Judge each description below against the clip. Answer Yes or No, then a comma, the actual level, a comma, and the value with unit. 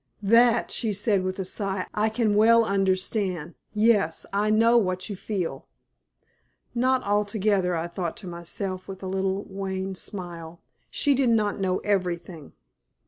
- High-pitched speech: Yes, high, 195 Hz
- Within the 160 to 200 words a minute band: No, average, 145 wpm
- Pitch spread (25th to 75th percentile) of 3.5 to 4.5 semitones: No, average, 2.7 semitones